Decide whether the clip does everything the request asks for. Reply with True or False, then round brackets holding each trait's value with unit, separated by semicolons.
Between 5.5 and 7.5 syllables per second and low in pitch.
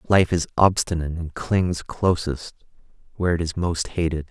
False (4.9 syllables/s; 85 Hz)